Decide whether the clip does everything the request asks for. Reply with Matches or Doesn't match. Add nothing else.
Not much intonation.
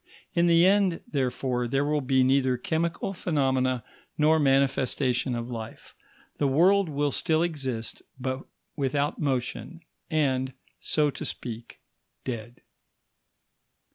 Doesn't match